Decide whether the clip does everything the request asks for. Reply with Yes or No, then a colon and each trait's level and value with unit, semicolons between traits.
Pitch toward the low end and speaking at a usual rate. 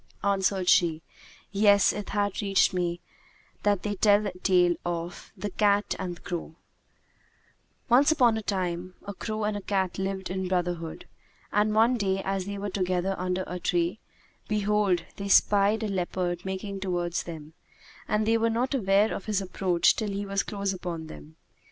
No: high, 195 Hz; average, 170 wpm